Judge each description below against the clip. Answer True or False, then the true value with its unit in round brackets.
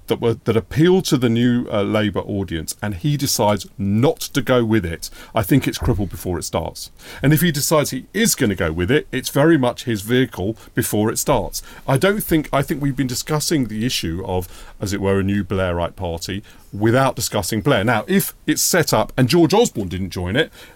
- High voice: False (115 Hz)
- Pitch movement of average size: False (6.1 semitones)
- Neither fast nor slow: False (220 wpm)